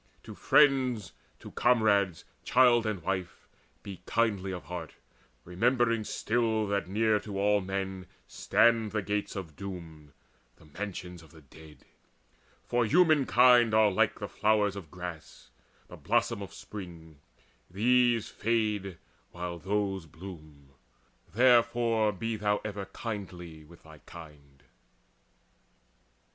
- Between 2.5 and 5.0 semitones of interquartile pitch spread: Yes, average, 4.4 semitones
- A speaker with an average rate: No, slow, 120 wpm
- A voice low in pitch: Yes, low, 100 Hz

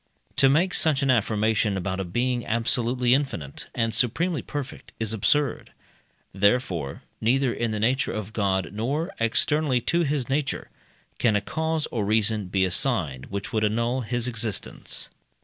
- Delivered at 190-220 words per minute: No, average, 150 wpm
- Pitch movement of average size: Yes, average, 4.4 semitones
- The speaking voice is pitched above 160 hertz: No, low, 115 Hz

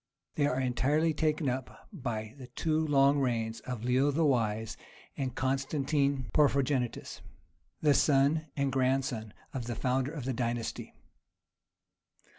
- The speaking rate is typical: No, slow, 130 wpm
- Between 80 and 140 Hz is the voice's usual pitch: Yes, low, 135 Hz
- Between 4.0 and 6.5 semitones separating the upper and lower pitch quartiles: No, average, 2.7 semitones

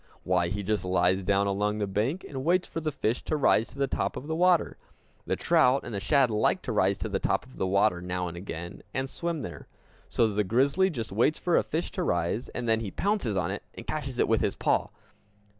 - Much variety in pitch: Yes, wide, 6.7 semitones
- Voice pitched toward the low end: Yes, low, 115 Hz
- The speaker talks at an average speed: No, fast, 240 wpm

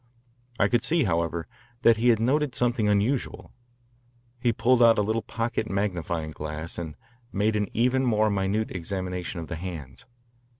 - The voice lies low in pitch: Yes, low, 105 Hz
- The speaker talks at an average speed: Yes, average, 160 wpm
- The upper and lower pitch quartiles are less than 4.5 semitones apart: No, average, 5.3 semitones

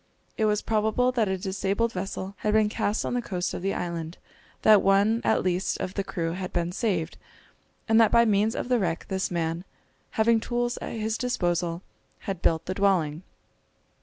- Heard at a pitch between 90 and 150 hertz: No, high, 195 Hz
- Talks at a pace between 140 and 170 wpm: No, average, 190 wpm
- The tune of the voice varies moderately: Yes, average, 3.7 semitones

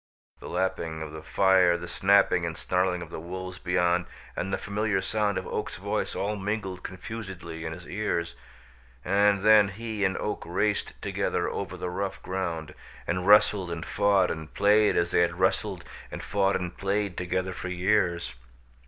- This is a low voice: Yes, very low, 95 Hz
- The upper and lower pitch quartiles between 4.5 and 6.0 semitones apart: No, narrow, 2.5 semitones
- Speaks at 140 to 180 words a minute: Yes, average, 170 wpm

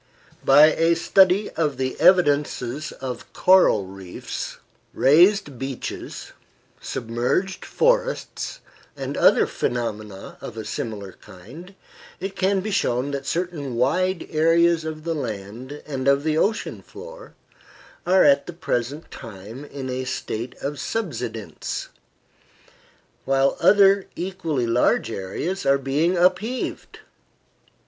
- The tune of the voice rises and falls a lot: Yes, wide, 6.7 semitones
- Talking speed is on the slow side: Yes, slow, 120 wpm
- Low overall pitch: No, medium, 145 Hz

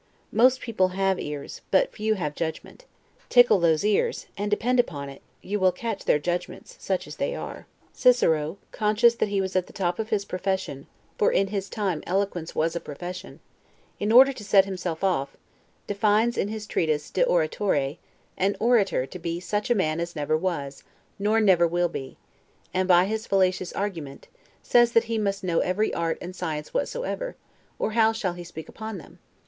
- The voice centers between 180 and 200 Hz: Yes, high, 190 Hz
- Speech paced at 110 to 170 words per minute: No, average, 185 wpm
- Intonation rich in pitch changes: No, average, 4.0 semitones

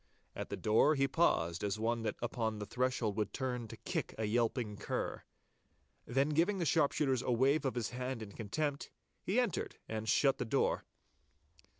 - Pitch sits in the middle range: No, low, 120 Hz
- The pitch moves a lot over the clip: No, average, 3.8 semitones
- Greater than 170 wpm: Yes, average, 180 wpm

